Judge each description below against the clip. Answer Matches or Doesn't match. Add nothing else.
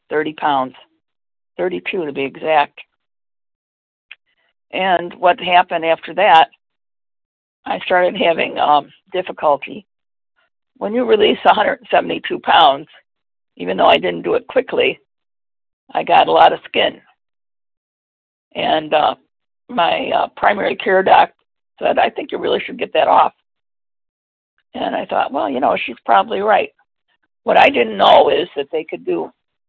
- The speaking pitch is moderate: Matches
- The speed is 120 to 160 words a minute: Matches